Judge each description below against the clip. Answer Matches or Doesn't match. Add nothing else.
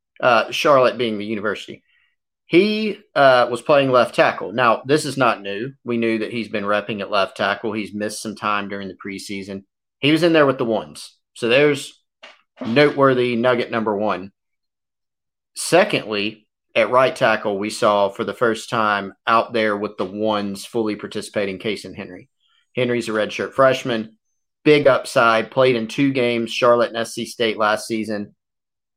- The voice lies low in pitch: Matches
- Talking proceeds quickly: Doesn't match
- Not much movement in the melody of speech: Doesn't match